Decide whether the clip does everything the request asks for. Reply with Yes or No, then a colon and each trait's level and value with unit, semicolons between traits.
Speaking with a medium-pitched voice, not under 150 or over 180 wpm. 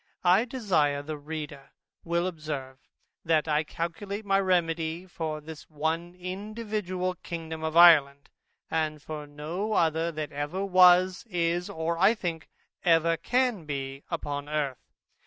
No: medium, 165 Hz; slow, 135 wpm